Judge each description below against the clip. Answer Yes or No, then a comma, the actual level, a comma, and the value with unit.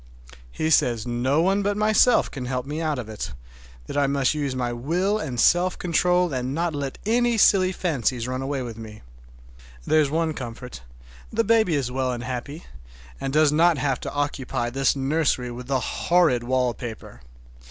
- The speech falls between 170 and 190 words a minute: Yes, average, 175 wpm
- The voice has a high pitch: No, medium, 140 Hz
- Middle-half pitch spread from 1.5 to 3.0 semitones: No, average, 5.1 semitones